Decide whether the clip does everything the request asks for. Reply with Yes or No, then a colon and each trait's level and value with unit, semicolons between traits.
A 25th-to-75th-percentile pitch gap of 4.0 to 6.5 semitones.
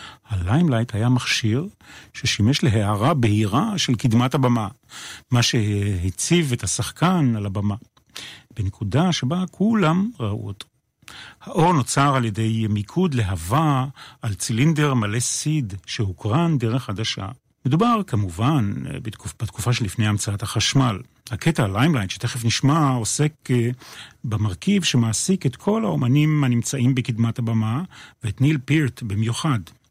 Yes: average, 5.1 semitones